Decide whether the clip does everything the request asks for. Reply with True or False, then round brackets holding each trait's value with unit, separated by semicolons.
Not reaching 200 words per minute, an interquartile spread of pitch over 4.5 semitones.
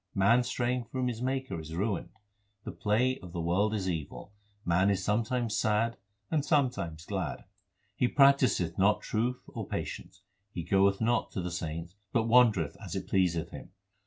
True (170 wpm; 5.6 semitones)